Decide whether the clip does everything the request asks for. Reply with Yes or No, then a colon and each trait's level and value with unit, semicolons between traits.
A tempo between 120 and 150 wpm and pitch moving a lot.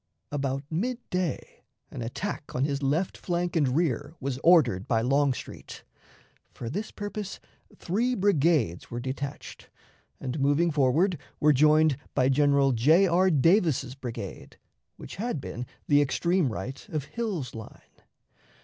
No: slow, 135 wpm; average, 4.9 semitones